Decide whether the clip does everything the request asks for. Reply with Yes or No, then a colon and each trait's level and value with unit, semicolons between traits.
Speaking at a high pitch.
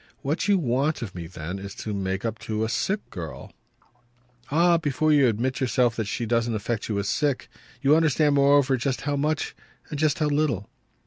No: low, 130 Hz